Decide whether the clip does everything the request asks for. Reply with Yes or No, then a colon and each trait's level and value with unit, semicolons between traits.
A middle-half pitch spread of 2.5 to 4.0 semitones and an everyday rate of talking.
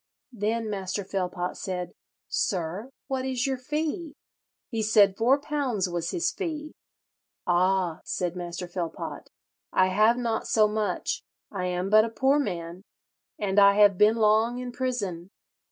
No: average, 5.2 semitones; average, 145 wpm